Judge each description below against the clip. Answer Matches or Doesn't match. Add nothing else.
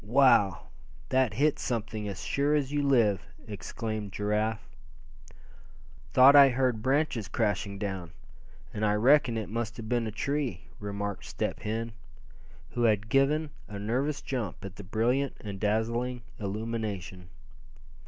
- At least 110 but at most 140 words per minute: Matches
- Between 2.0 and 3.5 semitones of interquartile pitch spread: Doesn't match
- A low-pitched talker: Matches